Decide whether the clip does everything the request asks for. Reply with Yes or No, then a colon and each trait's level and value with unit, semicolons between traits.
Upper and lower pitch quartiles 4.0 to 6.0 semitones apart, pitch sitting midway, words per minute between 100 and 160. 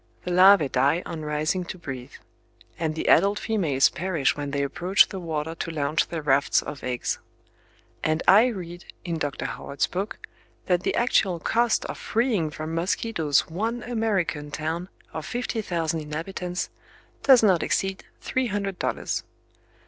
Yes: average, 4.3 semitones; medium, 170 Hz; average, 155 wpm